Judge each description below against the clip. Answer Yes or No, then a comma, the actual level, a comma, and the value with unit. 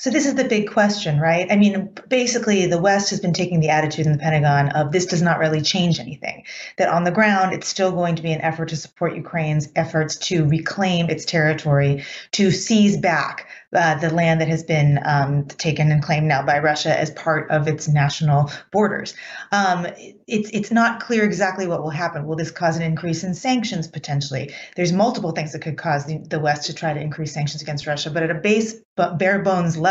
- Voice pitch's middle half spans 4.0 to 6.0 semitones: No, average, 3.6 semitones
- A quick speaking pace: Yes, fast, 220 wpm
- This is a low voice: No, medium, 165 Hz